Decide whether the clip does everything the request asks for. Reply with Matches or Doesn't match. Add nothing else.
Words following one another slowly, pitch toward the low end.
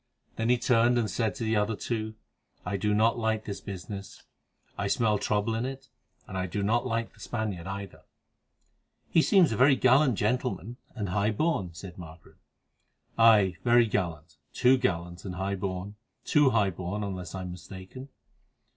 Doesn't match